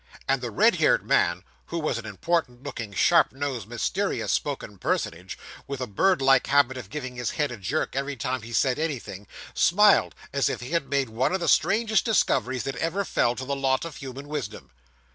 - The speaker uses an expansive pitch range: No, average, 4.2 semitones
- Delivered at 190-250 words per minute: Yes, average, 200 wpm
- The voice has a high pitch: No, low, 135 Hz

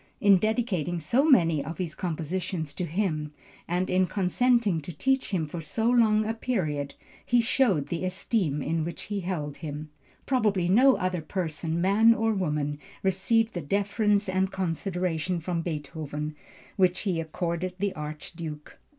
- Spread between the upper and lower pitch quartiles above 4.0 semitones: Yes, average, 4.4 semitones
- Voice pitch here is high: No, medium, 180 Hz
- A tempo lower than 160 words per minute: Yes, average, 150 wpm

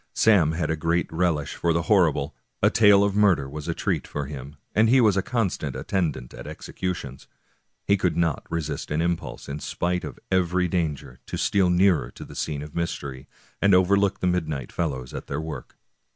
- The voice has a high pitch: No, very low, 85 Hz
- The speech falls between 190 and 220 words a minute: Yes, average, 195 wpm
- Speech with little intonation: No, average, 3.9 semitones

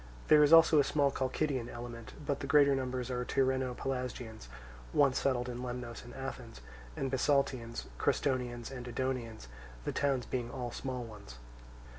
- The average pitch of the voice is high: No, low, 130 Hz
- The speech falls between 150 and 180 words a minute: Yes, average, 155 wpm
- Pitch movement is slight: Yes, narrow, 2.0 semitones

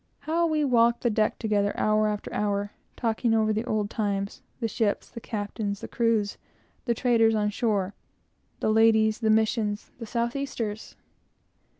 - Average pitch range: No, narrow, 2.0 semitones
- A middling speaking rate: Yes, average, 160 wpm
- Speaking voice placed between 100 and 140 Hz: No, high, 220 Hz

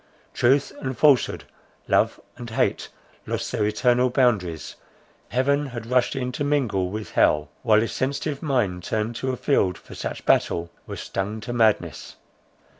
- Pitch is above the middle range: No, low, 120 Hz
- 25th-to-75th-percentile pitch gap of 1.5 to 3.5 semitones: No, average, 3.9 semitones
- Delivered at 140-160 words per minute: Yes, average, 150 wpm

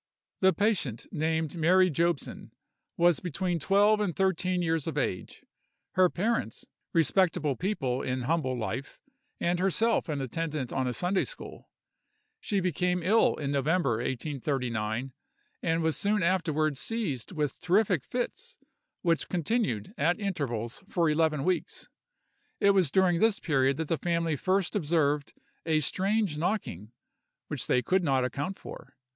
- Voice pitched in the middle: Yes, medium, 165 Hz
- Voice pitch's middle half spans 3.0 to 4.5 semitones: No, average, 5.0 semitones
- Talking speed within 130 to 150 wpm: Yes, average, 140 wpm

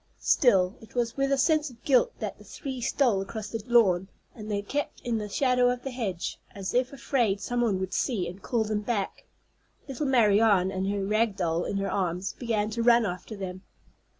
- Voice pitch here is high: Yes, high, 220 Hz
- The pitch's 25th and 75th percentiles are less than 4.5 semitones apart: Yes, average, 4.0 semitones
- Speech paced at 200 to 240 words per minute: Yes, fast, 205 wpm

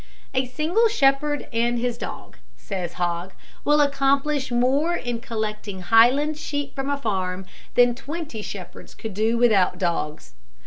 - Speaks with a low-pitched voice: No, high, 240 Hz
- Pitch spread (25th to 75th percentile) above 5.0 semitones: Yes, wide, 5.5 semitones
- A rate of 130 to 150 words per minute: Yes, average, 140 wpm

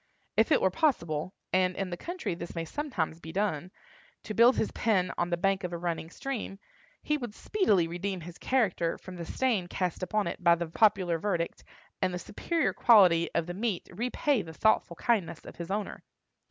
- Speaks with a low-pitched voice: No, medium, 185 Hz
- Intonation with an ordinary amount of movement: Yes, average, 4.2 semitones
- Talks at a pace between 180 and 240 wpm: Yes, average, 190 wpm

